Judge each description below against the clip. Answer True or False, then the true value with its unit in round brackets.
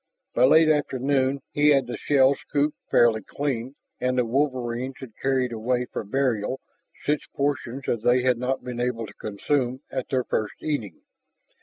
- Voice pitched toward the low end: True (130 Hz)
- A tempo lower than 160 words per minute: False (165 wpm)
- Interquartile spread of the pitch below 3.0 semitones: True (2.5 semitones)